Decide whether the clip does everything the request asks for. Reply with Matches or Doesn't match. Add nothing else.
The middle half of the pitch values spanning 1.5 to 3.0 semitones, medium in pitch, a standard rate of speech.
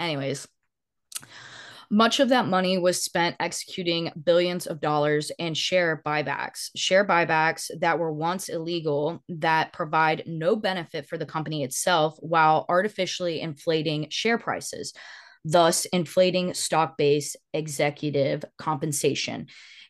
Doesn't match